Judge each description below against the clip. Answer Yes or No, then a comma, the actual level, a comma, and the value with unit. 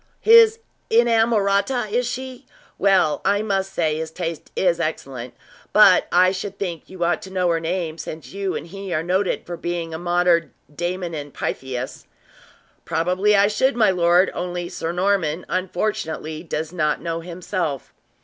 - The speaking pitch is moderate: Yes, medium, 180 Hz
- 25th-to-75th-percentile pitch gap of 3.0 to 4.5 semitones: Yes, average, 3.3 semitones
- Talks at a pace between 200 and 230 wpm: No, average, 160 wpm